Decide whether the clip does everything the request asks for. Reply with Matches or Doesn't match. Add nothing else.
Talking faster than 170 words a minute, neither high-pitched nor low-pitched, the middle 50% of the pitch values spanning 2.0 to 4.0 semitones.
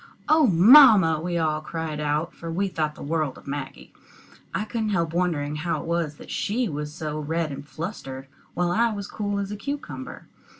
Doesn't match